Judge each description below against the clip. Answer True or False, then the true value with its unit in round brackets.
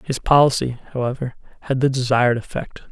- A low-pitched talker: True (130 Hz)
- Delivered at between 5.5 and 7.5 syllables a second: True (6.1 syllables/s)